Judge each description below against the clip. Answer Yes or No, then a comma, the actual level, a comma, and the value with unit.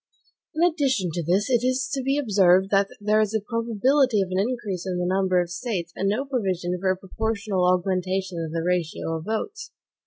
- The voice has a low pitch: No, high, 195 Hz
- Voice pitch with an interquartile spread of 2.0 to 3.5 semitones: No, average, 4.6 semitones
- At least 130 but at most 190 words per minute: No, fast, 205 wpm